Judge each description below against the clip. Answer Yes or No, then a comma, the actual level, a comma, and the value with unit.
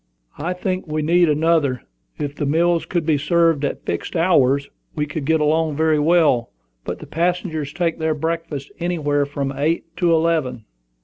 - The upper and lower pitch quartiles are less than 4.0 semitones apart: Yes, narrow, 2.6 semitones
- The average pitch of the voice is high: No, medium, 160 Hz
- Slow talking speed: No, average, 170 wpm